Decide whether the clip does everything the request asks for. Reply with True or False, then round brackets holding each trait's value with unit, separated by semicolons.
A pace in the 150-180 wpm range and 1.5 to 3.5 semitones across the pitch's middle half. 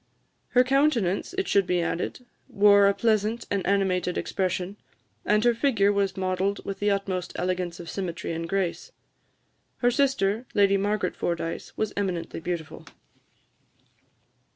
False (135 wpm; 2.8 semitones)